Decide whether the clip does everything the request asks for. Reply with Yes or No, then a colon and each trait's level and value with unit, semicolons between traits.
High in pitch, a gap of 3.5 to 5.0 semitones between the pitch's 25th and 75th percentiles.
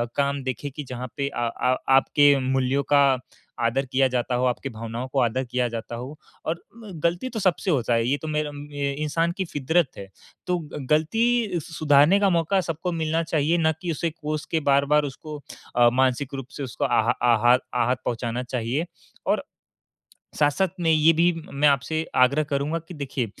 No: medium, 145 Hz; average, 4.2 semitones